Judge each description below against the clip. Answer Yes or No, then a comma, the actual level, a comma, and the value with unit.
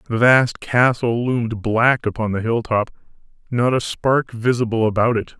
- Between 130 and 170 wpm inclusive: Yes, average, 155 wpm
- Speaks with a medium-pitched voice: No, low, 115 Hz